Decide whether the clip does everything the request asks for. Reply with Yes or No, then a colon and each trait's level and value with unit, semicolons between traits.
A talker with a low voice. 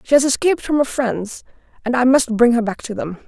No: very high, 250 Hz